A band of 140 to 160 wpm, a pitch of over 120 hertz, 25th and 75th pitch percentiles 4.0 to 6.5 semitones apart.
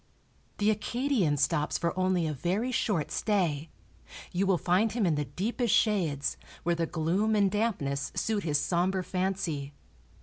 Yes: average, 155 wpm; medium, 185 Hz; average, 4.8 semitones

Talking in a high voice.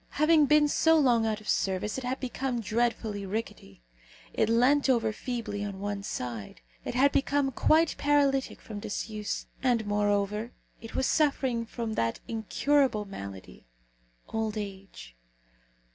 Yes: high, 225 Hz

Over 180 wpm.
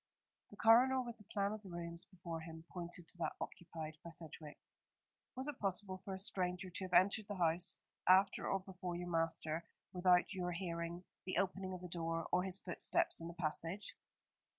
Yes: average, 190 wpm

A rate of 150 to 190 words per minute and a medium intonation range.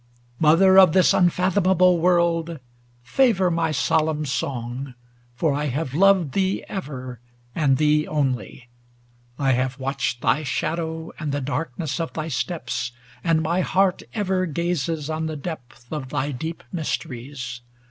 No: average, 140 wpm; average, 4.2 semitones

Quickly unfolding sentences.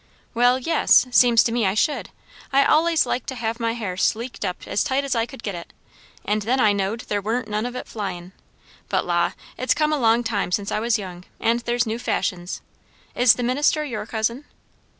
Yes: fast, 210 wpm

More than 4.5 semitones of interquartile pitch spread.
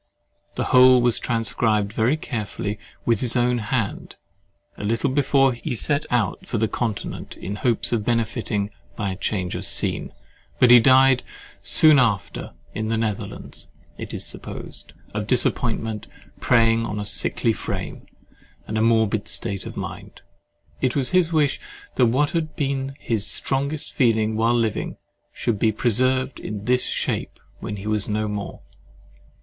No: average, 3.1 semitones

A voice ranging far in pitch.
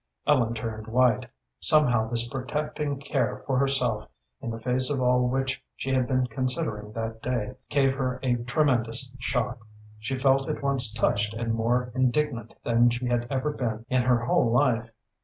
No: narrow, 2.5 semitones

